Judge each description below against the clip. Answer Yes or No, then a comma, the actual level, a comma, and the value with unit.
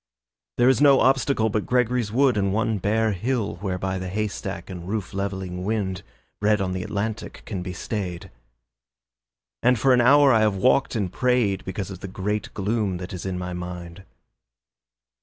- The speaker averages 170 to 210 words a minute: Yes, average, 175 wpm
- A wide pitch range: No, average, 3.4 semitones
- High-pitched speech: No, low, 100 Hz